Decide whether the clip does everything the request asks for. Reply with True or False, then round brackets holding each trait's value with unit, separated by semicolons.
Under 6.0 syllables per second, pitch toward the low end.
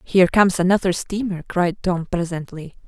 False (5.5 syllables/s; 180 Hz)